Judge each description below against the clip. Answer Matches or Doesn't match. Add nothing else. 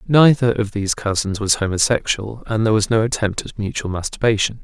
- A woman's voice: Doesn't match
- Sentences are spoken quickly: Doesn't match